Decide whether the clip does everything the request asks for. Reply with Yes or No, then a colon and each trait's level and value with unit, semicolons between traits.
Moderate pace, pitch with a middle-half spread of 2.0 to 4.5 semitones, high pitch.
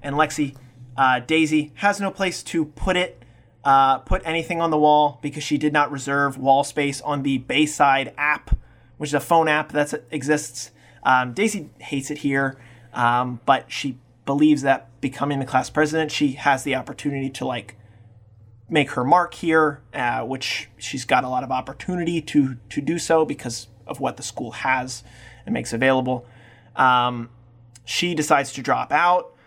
No: average, 175 wpm; average, 3.5 semitones; low, 135 Hz